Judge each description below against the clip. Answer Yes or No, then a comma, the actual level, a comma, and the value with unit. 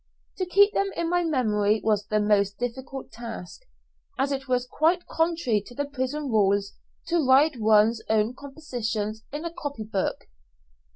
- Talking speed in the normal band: Yes, average, 160 wpm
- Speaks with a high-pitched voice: Yes, very high, 255 Hz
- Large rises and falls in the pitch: Yes, wide, 5.8 semitones